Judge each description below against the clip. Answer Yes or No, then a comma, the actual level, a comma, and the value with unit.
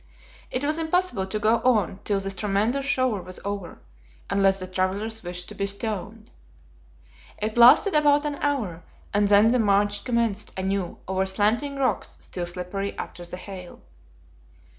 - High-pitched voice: Yes, high, 205 Hz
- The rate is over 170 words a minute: No, average, 155 wpm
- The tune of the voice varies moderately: Yes, average, 4.0 semitones